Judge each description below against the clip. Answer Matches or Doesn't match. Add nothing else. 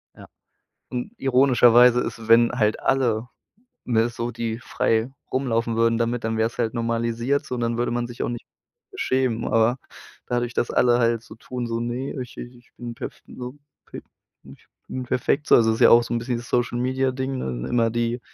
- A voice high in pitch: Doesn't match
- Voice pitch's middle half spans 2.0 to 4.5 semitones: Doesn't match